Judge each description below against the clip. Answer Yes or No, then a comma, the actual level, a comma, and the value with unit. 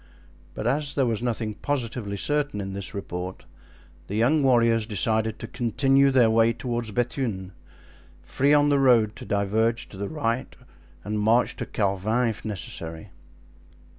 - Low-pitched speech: Yes, low, 115 Hz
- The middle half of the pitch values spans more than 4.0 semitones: No, average, 3.7 semitones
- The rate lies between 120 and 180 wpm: Yes, average, 150 wpm